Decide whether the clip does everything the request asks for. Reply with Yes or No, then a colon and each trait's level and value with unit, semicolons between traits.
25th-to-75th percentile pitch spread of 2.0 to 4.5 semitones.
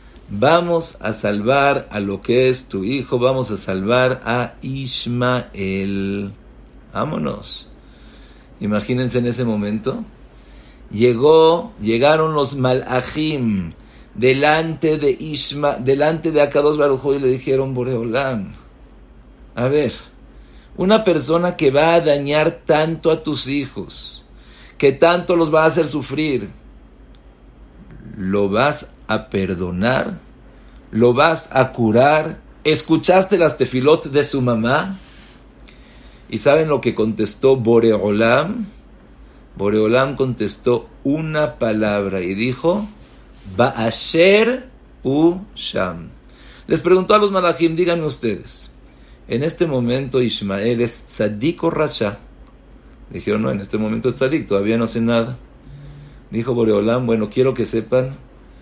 No: average, 5.3 semitones